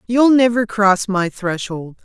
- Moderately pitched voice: No, high, 210 Hz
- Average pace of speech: Yes, average, 145 wpm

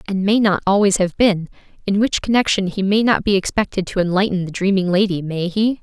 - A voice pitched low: No, high, 195 Hz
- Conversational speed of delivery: No, fast, 215 wpm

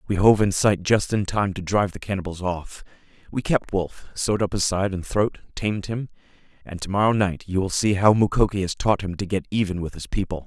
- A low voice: Yes, very low, 95 Hz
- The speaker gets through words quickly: Yes, fast, 230 wpm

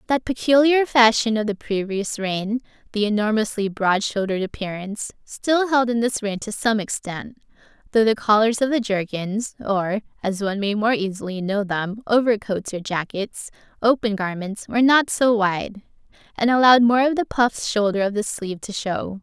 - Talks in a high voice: Yes, high, 215 Hz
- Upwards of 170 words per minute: No, average, 165 wpm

